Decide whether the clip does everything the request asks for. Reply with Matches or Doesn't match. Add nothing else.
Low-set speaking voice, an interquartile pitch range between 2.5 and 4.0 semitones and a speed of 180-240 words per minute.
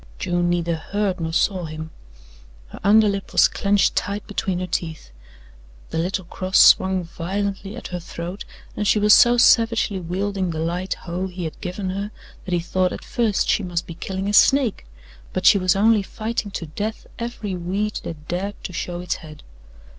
Doesn't match